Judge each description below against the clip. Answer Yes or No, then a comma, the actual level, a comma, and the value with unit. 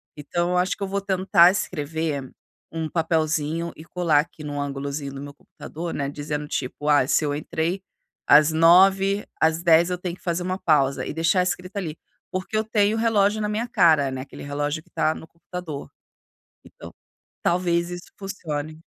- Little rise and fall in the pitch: No, average, 3.7 semitones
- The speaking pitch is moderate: Yes, medium, 165 Hz